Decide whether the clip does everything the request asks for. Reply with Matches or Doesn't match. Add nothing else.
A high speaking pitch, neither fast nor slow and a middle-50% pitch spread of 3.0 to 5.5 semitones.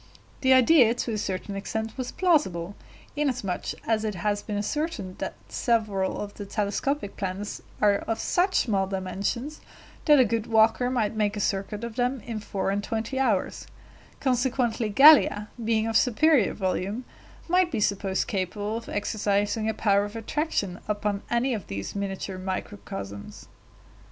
Matches